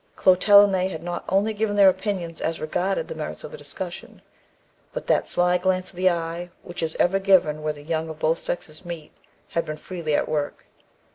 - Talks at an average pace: No, fast, 210 wpm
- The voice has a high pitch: No, medium, 175 Hz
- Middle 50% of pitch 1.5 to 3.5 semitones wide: Yes, average, 2.9 semitones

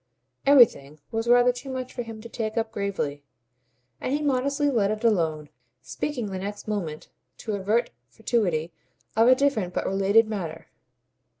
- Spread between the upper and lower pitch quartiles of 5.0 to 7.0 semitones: No, average, 4.3 semitones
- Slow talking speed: No, average, 165 wpm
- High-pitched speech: Yes, high, 220 Hz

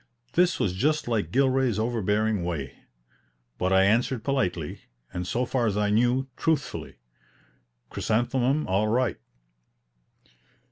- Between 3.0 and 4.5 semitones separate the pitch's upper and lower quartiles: No, average, 5.1 semitones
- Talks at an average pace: No, slow, 120 wpm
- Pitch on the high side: No, low, 115 Hz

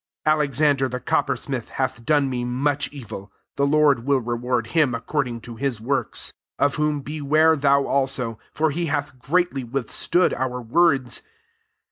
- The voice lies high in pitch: No, medium, 140 Hz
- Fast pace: No, average, 155 wpm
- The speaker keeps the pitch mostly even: No, average, 3.2 semitones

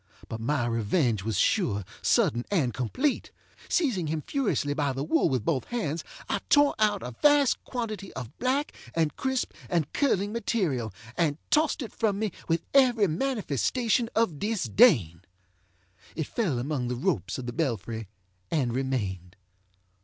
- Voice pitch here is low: No, medium, 160 Hz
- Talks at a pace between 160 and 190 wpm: No, average, 150 wpm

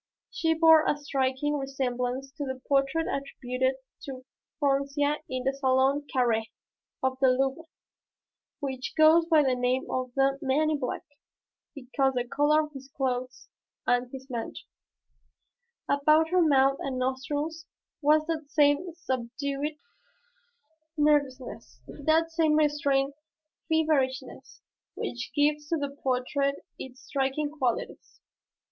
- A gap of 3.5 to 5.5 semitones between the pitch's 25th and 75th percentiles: No, narrow, 2.5 semitones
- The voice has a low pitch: No, very high, 275 Hz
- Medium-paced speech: No, slow, 125 wpm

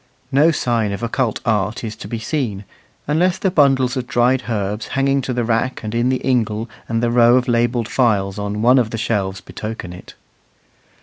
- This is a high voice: No, low, 120 Hz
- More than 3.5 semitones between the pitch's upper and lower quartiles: No, average, 3.1 semitones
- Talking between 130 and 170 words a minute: No, average, 195 wpm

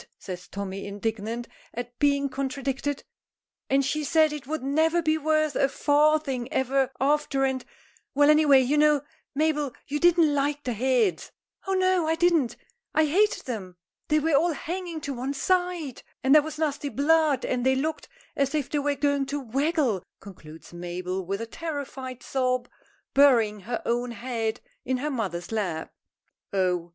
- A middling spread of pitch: Yes, average, 4.2 semitones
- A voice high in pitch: Yes, very high, 275 Hz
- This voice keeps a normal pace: Yes, average, 165 wpm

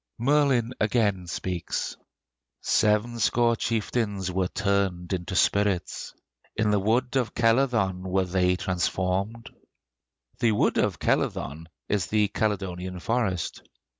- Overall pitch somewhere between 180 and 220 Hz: No, low, 100 Hz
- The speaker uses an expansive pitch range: No, average, 3.8 semitones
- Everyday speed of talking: No, slow, 105 wpm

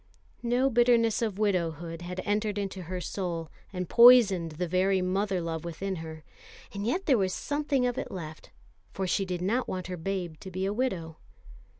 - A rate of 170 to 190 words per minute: Yes, average, 185 wpm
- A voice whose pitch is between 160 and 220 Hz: Yes, high, 190 Hz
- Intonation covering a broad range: No, average, 3.7 semitones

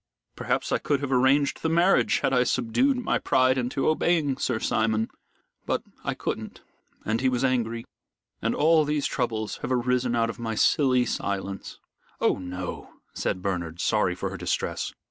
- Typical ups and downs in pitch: Yes, average, 4.0 semitones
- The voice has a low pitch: Yes, low, 125 Hz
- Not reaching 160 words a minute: No, average, 165 wpm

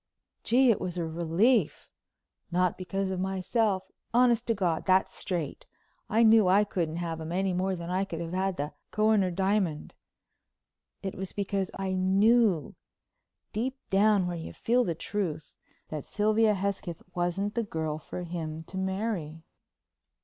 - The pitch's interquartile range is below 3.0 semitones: No, average, 3.4 semitones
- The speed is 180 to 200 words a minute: No, average, 150 wpm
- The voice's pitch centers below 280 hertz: Yes, high, 190 Hz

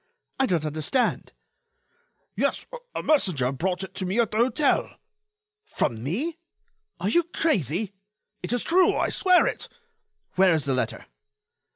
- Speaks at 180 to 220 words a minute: No, average, 140 wpm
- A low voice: No, high, 195 Hz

